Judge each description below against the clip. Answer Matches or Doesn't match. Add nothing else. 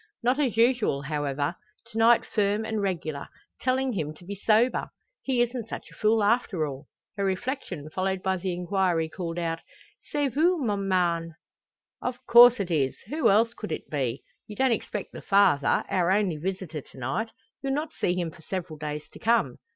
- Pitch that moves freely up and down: Matches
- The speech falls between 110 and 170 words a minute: Doesn't match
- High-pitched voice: Matches